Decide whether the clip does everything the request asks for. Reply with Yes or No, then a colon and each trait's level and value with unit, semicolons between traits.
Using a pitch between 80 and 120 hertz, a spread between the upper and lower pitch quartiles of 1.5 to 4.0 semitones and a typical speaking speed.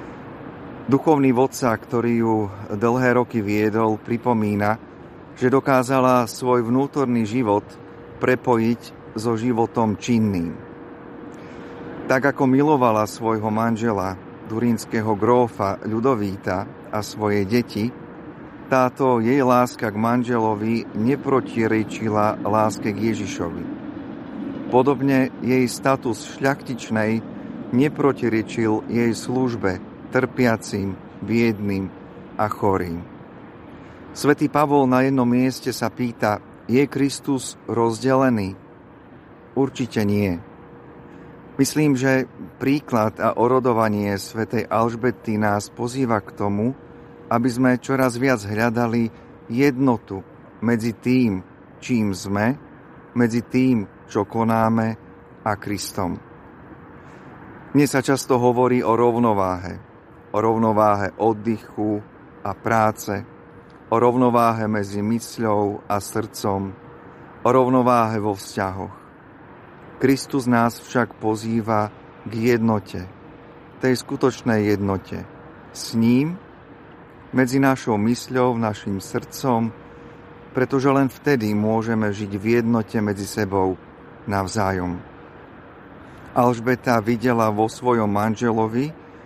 No: low, 115 Hz; average, 3.2 semitones; slow, 95 wpm